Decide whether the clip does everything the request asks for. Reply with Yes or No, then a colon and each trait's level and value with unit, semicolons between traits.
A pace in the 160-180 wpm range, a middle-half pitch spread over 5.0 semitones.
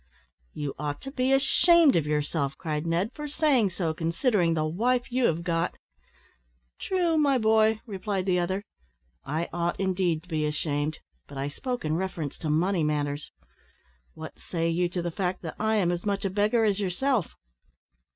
Yes: average, 175 wpm; wide, 5.6 semitones